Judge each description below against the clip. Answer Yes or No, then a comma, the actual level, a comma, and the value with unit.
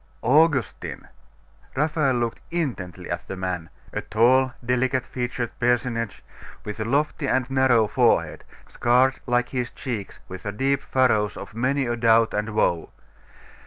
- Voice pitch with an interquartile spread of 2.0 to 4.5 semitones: Yes, average, 3.2 semitones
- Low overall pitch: Yes, low, 120 Hz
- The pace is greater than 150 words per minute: No, average, 140 wpm